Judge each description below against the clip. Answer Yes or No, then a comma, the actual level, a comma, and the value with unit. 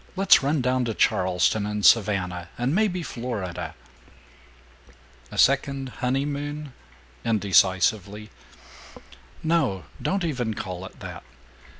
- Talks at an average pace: No, slow, 100 wpm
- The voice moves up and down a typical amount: No, wide, 6.7 semitones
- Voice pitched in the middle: No, low, 115 Hz